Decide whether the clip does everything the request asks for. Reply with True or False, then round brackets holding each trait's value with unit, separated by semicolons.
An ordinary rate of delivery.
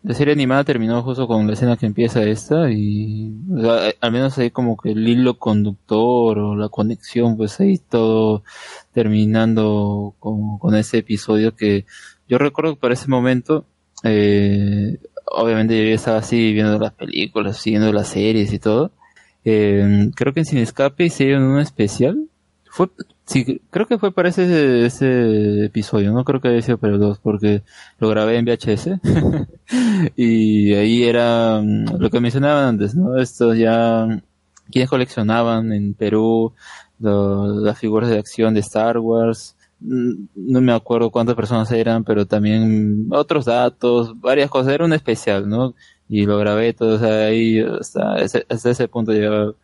True (165 wpm)